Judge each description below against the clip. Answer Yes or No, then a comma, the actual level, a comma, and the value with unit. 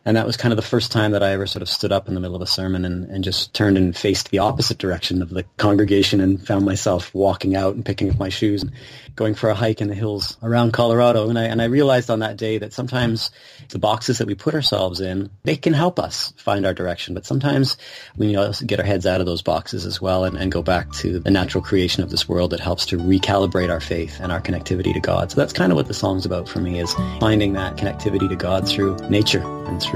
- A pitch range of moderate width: Yes, average, 3.2 semitones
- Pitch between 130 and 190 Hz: No, low, 100 Hz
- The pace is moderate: No, fast, 270 wpm